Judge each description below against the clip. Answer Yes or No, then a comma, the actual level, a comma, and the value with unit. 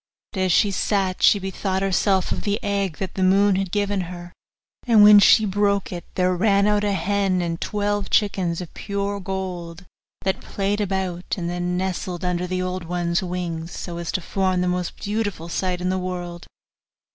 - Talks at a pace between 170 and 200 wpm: Yes, average, 190 wpm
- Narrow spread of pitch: Yes, narrow, 2.1 semitones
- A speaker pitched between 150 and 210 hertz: Yes, medium, 185 Hz